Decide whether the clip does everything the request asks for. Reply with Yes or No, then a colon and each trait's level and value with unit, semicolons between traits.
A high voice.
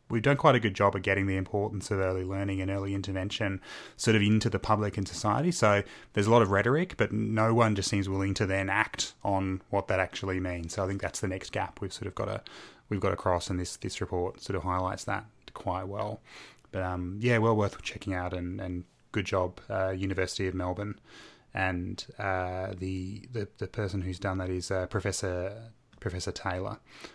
No: low, 100 Hz